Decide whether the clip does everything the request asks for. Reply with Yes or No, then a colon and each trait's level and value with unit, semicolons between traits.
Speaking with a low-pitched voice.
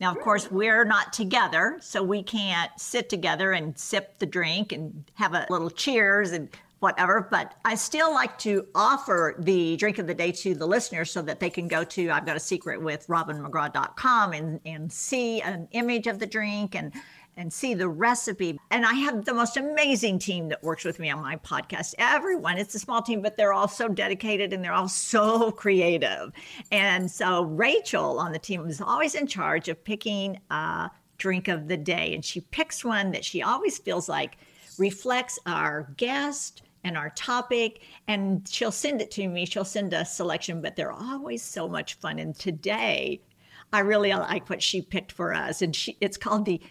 No: high, 195 Hz